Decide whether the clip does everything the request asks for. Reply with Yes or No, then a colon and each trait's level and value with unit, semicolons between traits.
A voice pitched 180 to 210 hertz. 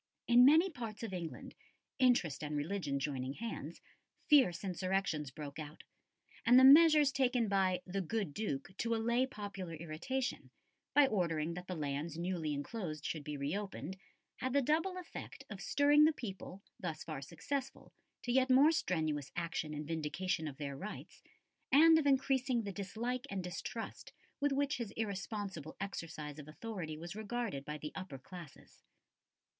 Yes: high, 190 Hz